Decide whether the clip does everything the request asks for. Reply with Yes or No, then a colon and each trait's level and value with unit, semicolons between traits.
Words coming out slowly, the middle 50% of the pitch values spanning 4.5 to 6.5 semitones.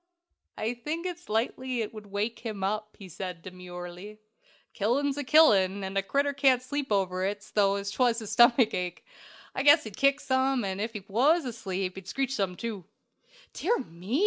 No: average, 175 wpm; average, 5.2 semitones